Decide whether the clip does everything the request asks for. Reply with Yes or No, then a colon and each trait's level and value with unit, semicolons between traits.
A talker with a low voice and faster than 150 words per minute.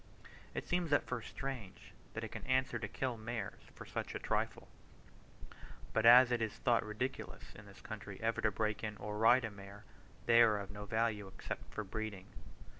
Yes: low, 110 Hz; average, 190 wpm